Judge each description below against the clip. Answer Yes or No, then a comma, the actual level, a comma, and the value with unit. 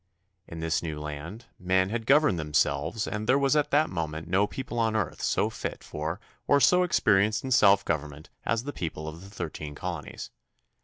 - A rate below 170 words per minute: No, average, 190 wpm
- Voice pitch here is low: Yes, very low, 95 Hz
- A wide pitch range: Yes, wide, 6.7 semitones